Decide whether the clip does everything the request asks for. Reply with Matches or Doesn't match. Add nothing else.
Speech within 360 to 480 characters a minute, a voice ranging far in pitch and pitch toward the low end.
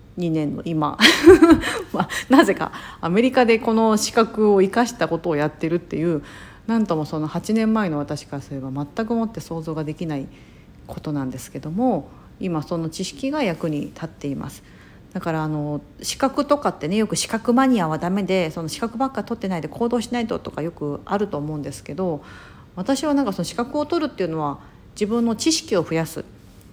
Doesn't match